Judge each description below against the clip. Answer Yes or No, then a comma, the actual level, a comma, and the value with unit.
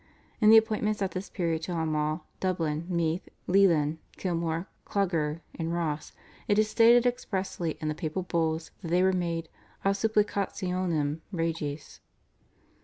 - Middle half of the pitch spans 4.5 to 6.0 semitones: No, average, 3.5 semitones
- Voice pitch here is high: No, medium, 170 Hz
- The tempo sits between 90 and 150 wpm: Yes, average, 140 wpm